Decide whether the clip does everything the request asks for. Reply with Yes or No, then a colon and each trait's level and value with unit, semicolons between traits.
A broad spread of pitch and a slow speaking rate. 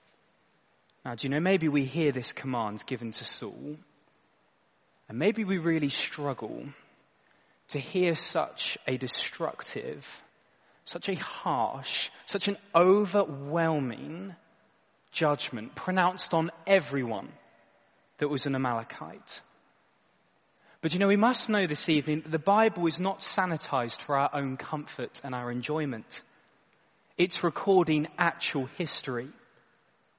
No: average, 5.0 semitones; slow, 120 wpm